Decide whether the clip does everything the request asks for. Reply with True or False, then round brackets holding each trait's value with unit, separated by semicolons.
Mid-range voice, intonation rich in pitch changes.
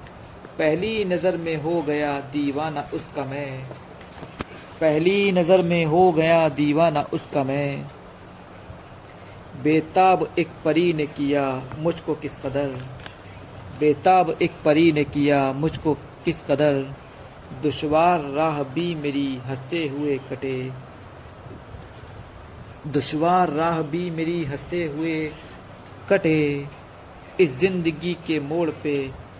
False (150 Hz; 3.1 semitones)